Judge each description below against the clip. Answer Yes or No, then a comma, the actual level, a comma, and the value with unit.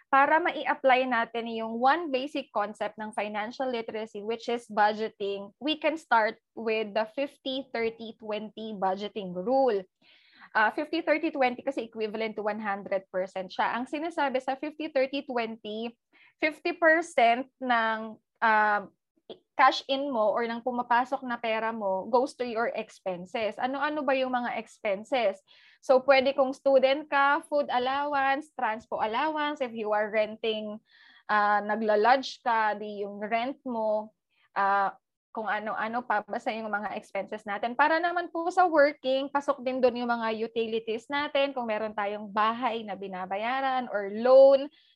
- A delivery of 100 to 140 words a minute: Yes, average, 135 wpm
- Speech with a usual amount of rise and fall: Yes, average, 4.2 semitones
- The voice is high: Yes, high, 235 Hz